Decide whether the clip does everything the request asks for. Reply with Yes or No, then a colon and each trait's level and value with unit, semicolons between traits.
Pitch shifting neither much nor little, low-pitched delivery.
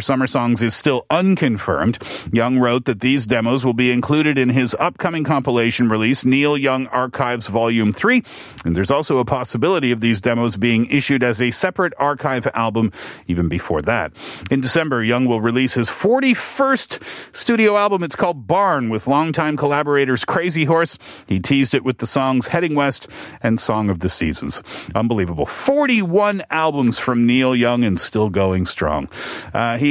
Yes: average, 4.2 semitones; low, 130 Hz